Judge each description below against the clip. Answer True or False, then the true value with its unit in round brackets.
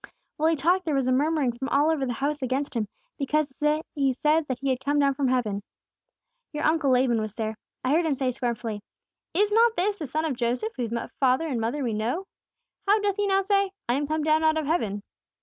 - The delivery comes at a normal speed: False (225 wpm)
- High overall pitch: True (280 Hz)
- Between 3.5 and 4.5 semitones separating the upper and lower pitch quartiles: True (4.2 semitones)